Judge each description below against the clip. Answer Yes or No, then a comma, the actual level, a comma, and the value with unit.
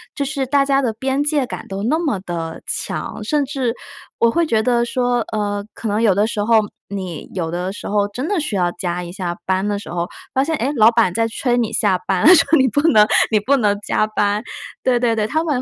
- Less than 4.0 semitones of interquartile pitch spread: No, average, 4.7 semitones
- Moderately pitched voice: No, high, 225 Hz